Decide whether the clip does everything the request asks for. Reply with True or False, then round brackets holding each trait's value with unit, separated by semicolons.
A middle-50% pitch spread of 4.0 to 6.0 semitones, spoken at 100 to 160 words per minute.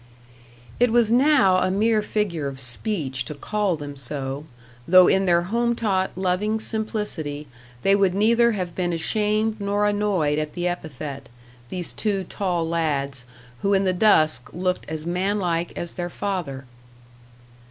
True (5.0 semitones; 155 wpm)